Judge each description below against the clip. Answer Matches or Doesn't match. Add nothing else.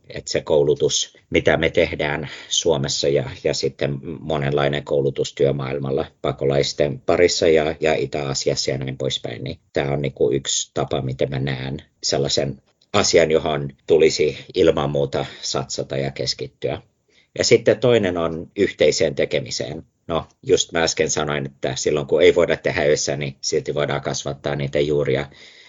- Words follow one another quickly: Doesn't match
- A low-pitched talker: Matches